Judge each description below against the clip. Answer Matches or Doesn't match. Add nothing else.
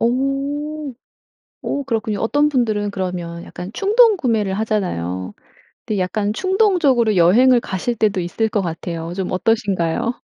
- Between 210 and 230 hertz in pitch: Matches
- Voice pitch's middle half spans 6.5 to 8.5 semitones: Matches